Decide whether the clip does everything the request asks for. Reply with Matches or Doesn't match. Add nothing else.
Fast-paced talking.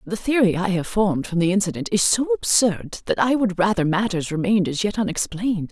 Matches